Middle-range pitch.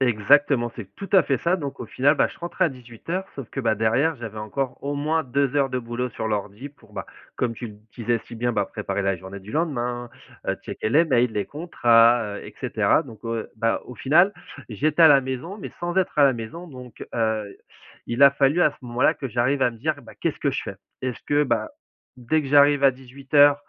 No: low, 125 Hz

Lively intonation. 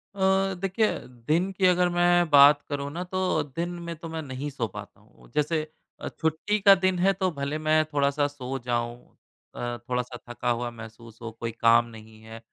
Yes: wide, 6.6 semitones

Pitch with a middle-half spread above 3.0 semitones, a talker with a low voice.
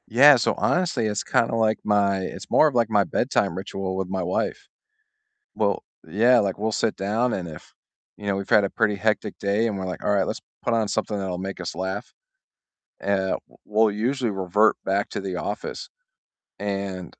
No: narrow, 2.4 semitones; low, 100 Hz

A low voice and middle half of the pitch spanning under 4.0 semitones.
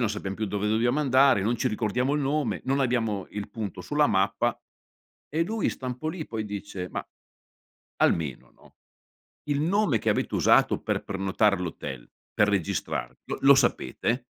No: low, 115 Hz; wide, 5.4 semitones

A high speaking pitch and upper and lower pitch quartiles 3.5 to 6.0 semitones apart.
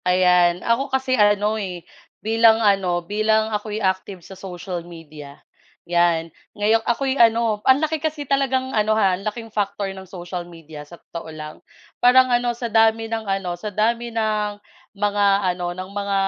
Yes: high, 205 Hz; average, 4.0 semitones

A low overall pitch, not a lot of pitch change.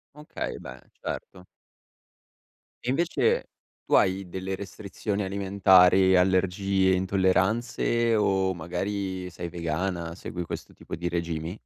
Yes: very low, 95 Hz; narrow, 1.7 semitones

